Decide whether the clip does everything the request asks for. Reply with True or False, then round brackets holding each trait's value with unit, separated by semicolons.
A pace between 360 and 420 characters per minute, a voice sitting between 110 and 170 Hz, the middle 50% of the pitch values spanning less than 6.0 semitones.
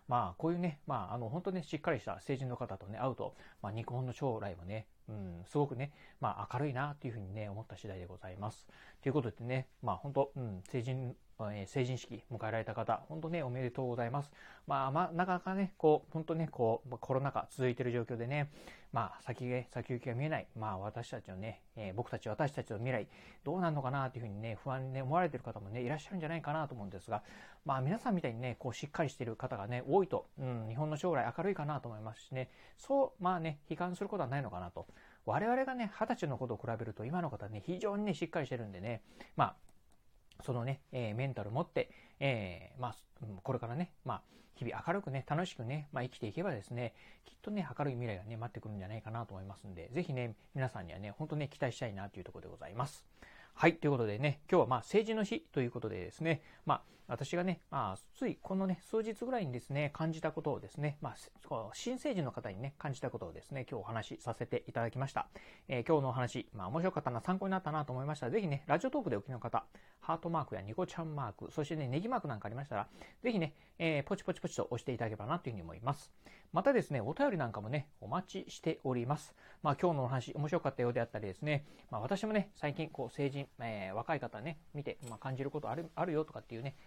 False (470 characters per minute; 135 Hz; 5.6 semitones)